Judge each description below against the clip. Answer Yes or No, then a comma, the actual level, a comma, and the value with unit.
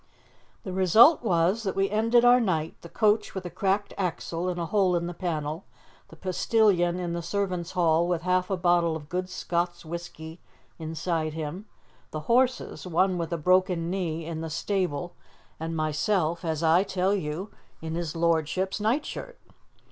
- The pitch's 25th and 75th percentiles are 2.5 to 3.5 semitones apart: Yes, average, 2.8 semitones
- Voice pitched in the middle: Yes, medium, 175 Hz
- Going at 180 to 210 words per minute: No, average, 170 wpm